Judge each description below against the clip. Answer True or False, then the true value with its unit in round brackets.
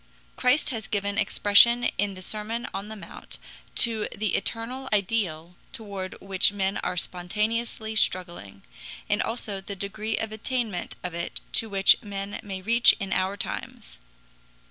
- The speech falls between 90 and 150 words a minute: True (145 wpm)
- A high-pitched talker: True (205 Hz)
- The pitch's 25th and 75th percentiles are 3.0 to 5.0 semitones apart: False (2.6 semitones)